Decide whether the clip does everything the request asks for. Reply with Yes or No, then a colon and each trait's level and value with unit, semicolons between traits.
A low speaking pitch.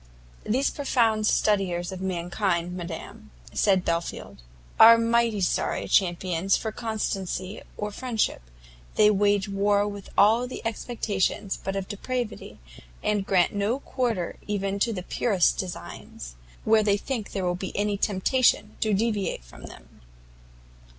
No: high, 205 Hz